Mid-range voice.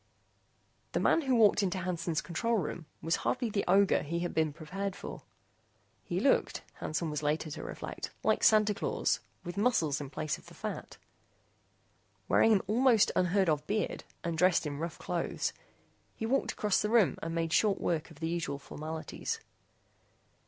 Yes: medium, 175 Hz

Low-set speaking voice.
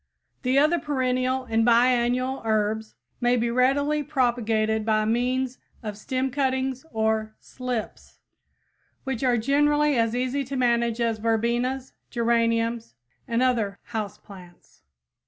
No: high, 240 Hz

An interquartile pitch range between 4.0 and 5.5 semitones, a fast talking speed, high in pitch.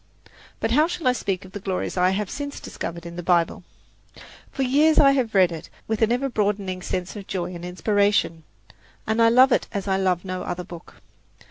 Yes: average, 4.6 semitones; fast, 210 wpm; high, 195 Hz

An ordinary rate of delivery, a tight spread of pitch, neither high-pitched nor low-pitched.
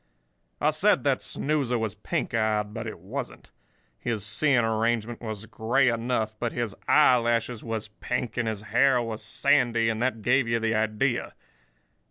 No: average, 165 wpm; narrow, 2.1 semitones; low, 115 Hz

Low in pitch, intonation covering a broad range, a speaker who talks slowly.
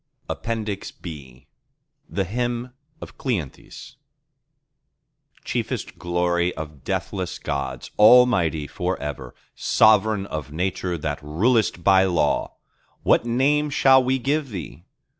Yes: very low, 95 Hz; wide, 7.2 semitones; slow, 105 wpm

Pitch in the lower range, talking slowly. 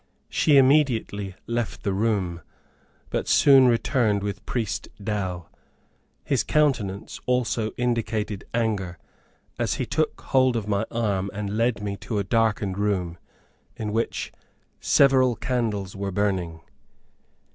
Yes: low, 105 Hz; slow, 125 wpm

